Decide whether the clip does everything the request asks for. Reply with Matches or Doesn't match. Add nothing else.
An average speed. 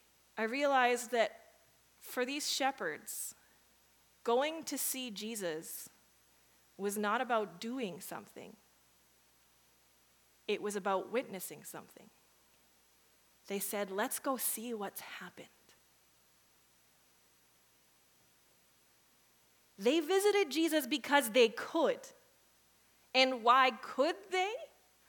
Doesn't match